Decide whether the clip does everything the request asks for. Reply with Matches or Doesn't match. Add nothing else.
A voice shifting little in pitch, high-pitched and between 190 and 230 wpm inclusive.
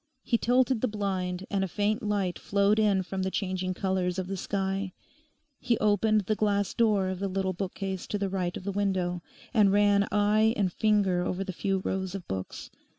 Matches